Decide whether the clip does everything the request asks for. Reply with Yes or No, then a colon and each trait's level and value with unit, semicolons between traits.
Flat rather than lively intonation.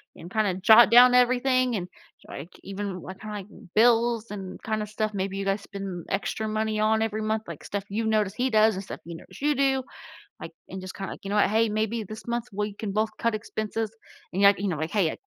Yes: narrow, 2.3 semitones